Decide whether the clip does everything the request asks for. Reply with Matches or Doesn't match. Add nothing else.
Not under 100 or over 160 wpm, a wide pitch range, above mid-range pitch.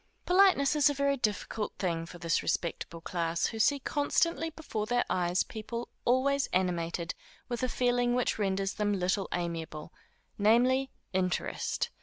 Matches